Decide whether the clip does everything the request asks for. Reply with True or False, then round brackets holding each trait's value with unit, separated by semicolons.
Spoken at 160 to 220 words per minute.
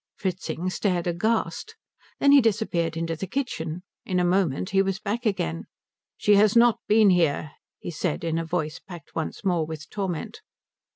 True (170 wpm)